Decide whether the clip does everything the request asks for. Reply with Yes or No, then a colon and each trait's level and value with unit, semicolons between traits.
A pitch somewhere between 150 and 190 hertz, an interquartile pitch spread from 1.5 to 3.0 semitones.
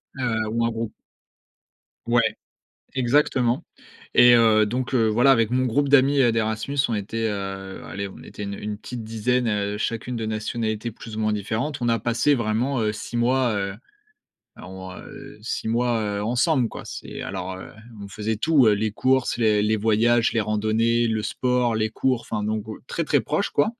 No: low, 115 Hz; narrow, 2.4 semitones